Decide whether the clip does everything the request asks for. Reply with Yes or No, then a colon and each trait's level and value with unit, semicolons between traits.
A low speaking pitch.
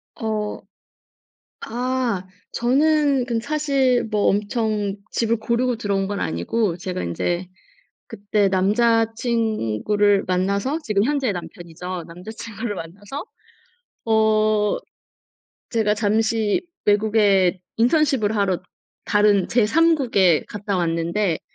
No: high, 210 Hz